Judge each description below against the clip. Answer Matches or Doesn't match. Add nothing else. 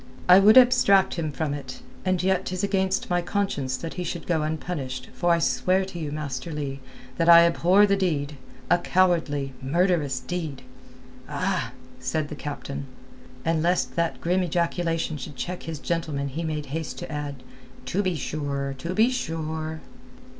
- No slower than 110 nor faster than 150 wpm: Doesn't match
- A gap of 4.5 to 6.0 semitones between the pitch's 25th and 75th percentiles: Doesn't match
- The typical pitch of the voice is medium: Matches